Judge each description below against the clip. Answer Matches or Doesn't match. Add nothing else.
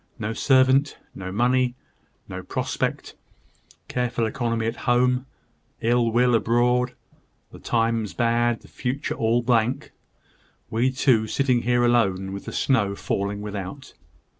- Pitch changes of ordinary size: Doesn't match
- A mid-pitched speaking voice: Doesn't match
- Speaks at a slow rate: Matches